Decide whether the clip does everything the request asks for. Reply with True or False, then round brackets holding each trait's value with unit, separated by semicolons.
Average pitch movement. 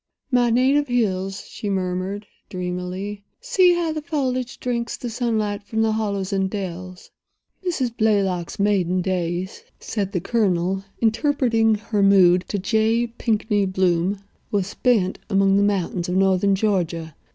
True (3.6 semitones)